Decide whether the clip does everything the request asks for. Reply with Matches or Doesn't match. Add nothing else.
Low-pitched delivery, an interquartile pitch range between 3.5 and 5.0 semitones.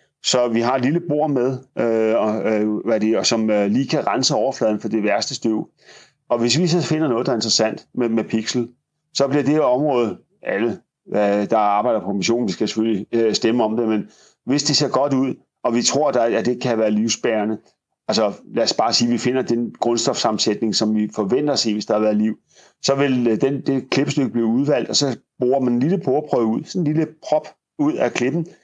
Matches